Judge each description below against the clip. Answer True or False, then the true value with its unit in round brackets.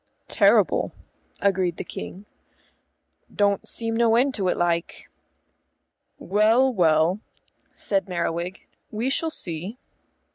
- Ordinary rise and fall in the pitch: True (4.6 semitones)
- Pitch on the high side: True (195 Hz)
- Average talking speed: False (105 wpm)